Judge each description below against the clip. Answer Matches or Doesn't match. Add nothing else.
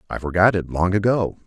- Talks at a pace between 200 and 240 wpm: Matches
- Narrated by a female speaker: Doesn't match